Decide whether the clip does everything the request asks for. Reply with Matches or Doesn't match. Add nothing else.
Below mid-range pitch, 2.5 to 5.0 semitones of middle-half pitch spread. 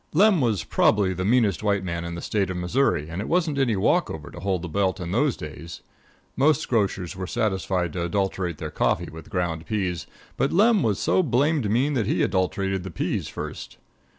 Doesn't match